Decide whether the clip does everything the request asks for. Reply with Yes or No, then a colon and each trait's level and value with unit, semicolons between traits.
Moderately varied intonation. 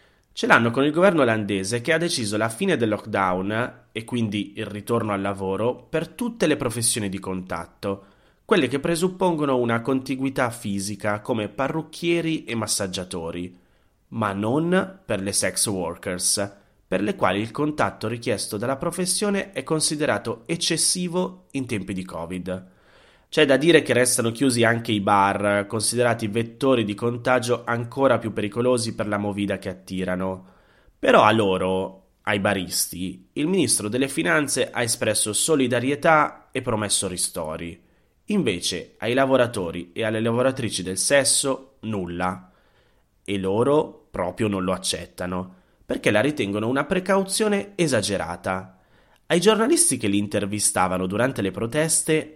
No: wide, 5.7 semitones